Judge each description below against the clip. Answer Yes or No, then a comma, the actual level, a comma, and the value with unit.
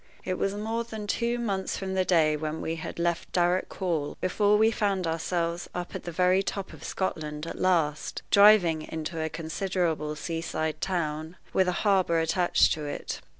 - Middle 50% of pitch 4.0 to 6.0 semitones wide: No, average, 3.3 semitones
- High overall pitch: No, medium, 175 Hz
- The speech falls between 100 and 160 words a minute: No, average, 185 wpm